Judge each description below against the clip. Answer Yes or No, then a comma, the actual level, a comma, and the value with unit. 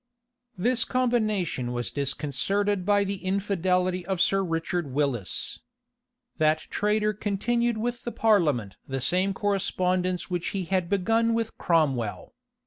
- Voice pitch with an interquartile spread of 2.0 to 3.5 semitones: No, average, 4.4 semitones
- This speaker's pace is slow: Yes, slow, 125 wpm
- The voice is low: No, medium, 185 Hz